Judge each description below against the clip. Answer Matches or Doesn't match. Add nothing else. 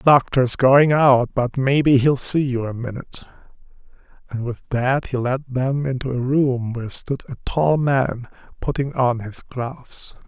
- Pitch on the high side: Doesn't match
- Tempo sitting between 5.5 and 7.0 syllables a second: Doesn't match